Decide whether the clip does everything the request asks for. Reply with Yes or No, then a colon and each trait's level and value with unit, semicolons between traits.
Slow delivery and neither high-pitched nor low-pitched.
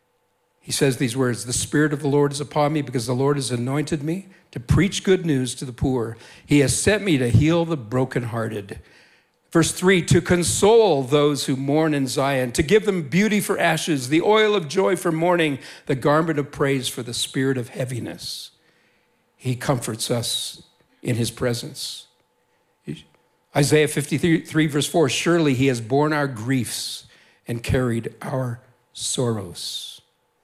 No: average, 165 wpm; medium, 145 Hz